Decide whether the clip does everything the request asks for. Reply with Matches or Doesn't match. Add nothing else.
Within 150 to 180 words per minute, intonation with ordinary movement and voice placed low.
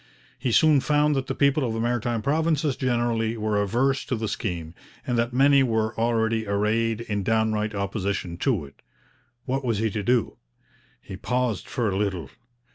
Matches